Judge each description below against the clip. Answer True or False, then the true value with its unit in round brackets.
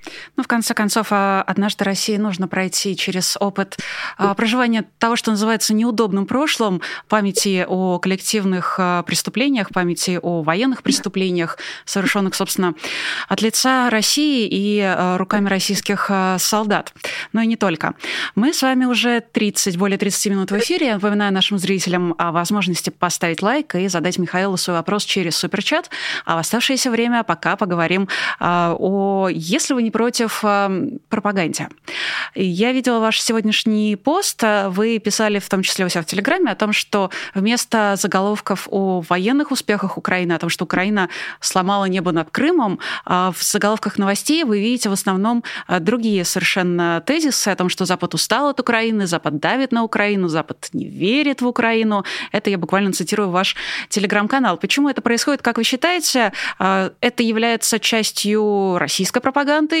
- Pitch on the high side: True (205 Hz)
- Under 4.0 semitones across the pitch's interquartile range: True (3.6 semitones)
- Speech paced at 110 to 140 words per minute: False (150 wpm)